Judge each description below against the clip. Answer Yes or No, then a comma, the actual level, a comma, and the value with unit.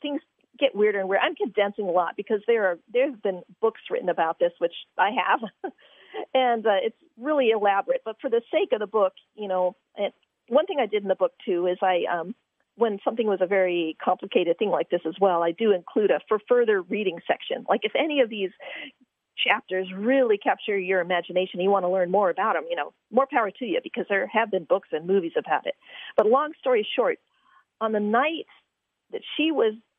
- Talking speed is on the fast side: Yes, fast, 220 wpm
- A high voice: Yes, high, 215 Hz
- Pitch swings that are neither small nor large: No, wide, 6.1 semitones